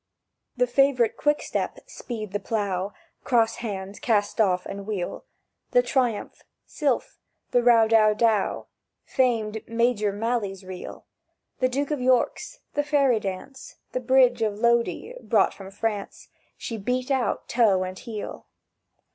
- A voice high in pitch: Yes, high, 225 Hz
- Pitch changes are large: No, average, 3.5 semitones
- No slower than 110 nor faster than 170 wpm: Yes, average, 140 wpm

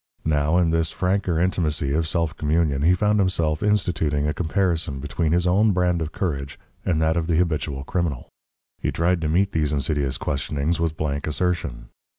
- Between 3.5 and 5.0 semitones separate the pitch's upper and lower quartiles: No, average, 3.1 semitones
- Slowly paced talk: No, average, 175 wpm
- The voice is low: Yes, very low, 80 Hz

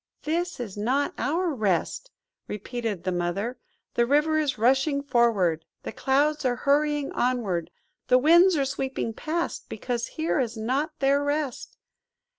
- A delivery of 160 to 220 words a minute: No, average, 140 wpm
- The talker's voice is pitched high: Yes, very high, 265 Hz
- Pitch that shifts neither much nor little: Yes, average, 4.6 semitones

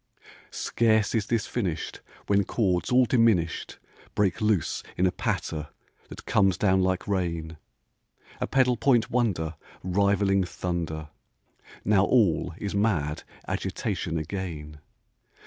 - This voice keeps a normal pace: No, slow, 115 wpm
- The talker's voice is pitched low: Yes, very low, 95 Hz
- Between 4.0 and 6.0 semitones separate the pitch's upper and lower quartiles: Yes, average, 4.4 semitones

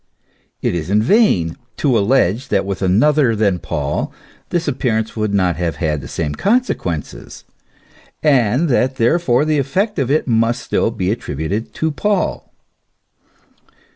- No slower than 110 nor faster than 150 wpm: Yes, average, 145 wpm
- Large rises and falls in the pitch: Yes, wide, 7.5 semitones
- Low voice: Yes, low, 115 Hz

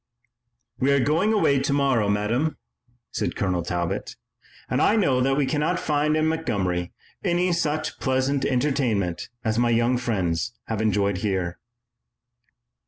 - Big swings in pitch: Yes, wide, 6.5 semitones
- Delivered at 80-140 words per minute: Yes, slow, 135 wpm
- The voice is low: Yes, low, 125 Hz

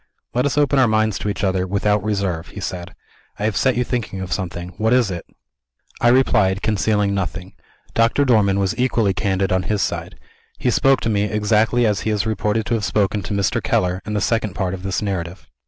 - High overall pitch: No, low, 105 Hz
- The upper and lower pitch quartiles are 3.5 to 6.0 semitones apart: No, average, 2.8 semitones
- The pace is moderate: No, fast, 215 wpm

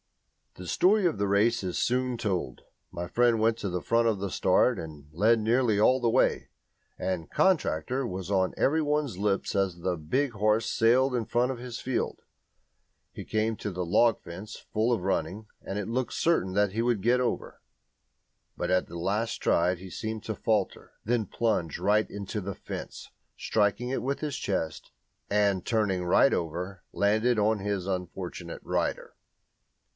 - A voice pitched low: Yes, low, 105 Hz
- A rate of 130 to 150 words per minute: No, average, 175 wpm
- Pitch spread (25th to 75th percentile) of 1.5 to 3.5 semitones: No, average, 4.2 semitones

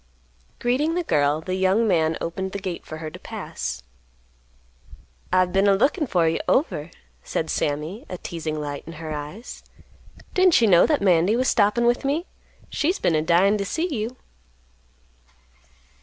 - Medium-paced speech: Yes, average, 165 wpm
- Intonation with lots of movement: Yes, wide, 6.9 semitones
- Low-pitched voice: No, high, 190 Hz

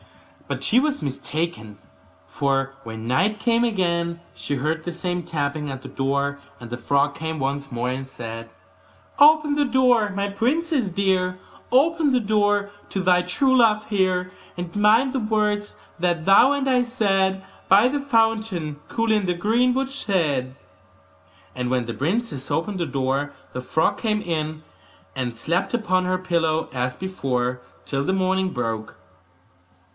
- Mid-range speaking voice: Yes, medium, 180 Hz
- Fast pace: No, average, 155 wpm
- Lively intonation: Yes, wide, 7.6 semitones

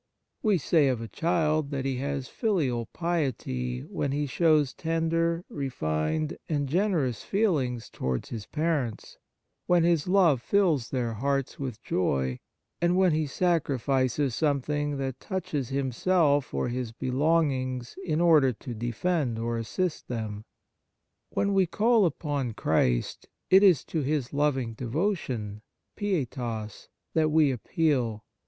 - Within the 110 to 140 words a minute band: Yes, slow, 135 wpm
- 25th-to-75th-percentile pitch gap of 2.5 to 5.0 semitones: No, wide, 5.4 semitones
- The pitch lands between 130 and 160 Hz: Yes, medium, 140 Hz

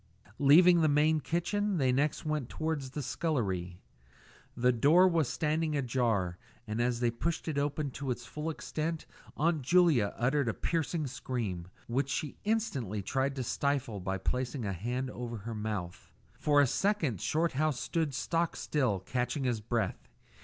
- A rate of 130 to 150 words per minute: No, average, 160 wpm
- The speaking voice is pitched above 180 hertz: No, low, 135 Hz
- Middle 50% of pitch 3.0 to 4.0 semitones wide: No, average, 4.8 semitones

